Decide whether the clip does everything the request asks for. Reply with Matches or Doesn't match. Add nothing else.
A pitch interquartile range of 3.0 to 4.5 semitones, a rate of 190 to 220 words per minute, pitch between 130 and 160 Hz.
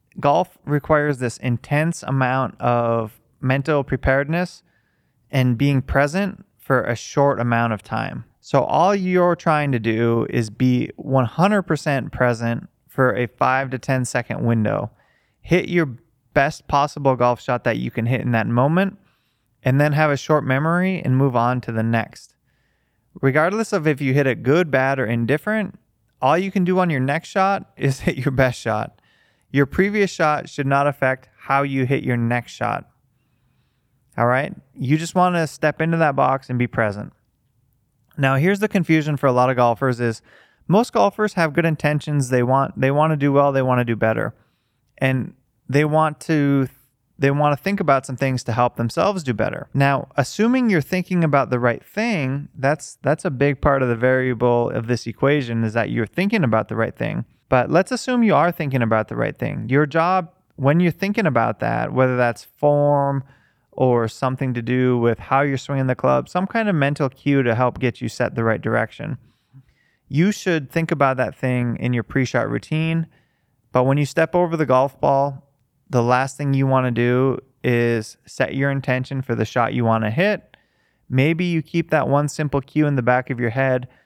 Matches